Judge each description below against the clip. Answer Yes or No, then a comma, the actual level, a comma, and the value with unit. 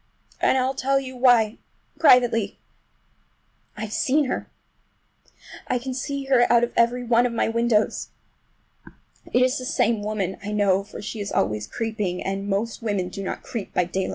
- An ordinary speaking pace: Yes, average, 160 wpm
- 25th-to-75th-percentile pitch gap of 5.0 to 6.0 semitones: No, average, 3.7 semitones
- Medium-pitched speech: No, high, 230 Hz